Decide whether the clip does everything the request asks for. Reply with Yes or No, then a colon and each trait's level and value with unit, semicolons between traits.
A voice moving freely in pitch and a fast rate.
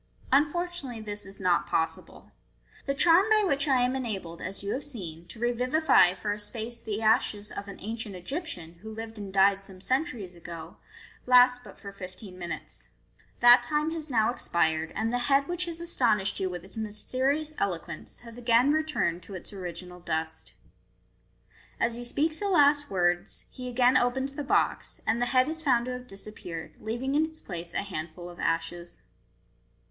No: wide, 6.5 semitones; average, 180 wpm